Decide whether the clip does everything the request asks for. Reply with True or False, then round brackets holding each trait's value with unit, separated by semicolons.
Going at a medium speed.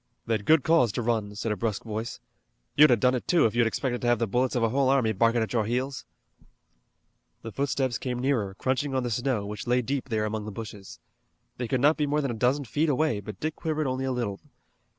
False (240 wpm)